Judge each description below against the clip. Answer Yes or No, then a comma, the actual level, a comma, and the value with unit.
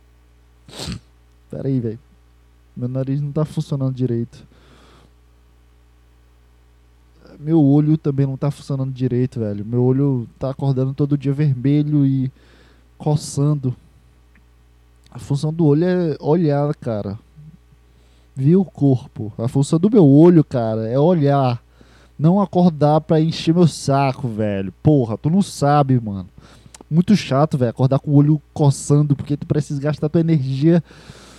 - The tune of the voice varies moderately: No, wide, 8.5 semitones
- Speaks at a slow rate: No, average, 135 wpm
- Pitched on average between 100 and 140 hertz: Yes, low, 135 Hz